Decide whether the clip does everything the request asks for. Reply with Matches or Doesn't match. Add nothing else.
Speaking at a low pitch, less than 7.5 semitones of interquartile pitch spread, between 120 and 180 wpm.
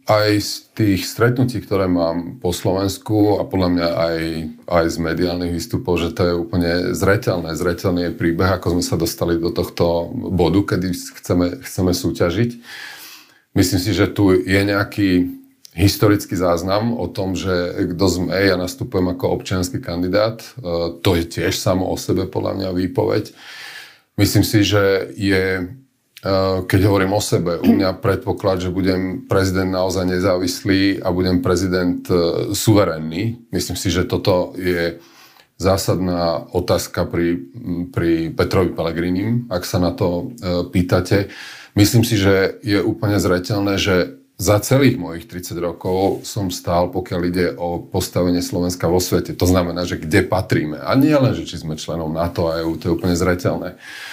Matches